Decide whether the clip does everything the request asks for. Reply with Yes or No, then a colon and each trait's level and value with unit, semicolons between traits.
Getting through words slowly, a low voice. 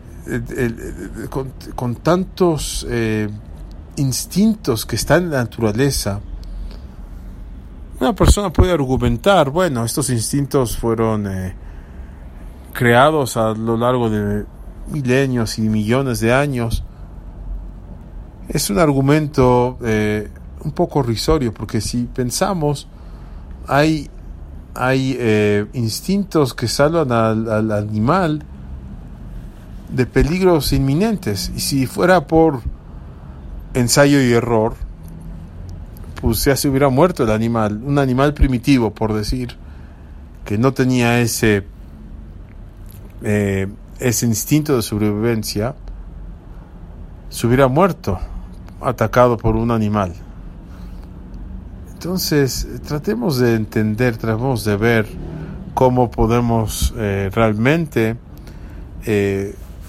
Yes: slow, 100 wpm; low, 110 Hz